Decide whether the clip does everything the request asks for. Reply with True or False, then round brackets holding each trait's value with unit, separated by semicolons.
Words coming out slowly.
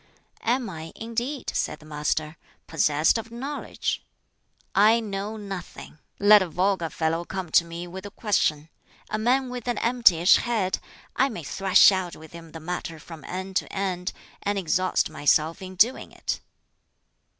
False (160 wpm)